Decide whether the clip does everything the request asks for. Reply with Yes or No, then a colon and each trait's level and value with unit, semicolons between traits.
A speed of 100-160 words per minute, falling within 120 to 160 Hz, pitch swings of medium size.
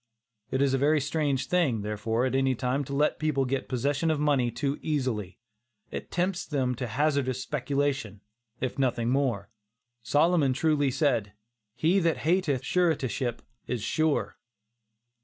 Yes: average, 145 wpm; low, 135 Hz; average, 3.2 semitones